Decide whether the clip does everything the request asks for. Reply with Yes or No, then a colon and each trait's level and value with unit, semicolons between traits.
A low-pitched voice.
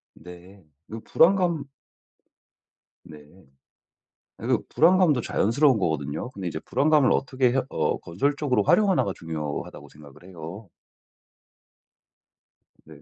Yes: low, 105 Hz